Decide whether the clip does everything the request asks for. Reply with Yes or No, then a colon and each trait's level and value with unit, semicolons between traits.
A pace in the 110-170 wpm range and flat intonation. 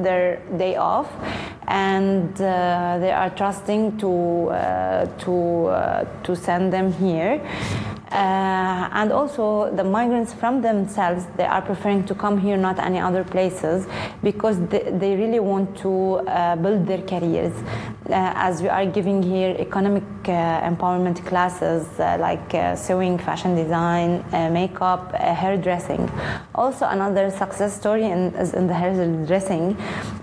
Yes: average, 145 wpm; narrow, 1.9 semitones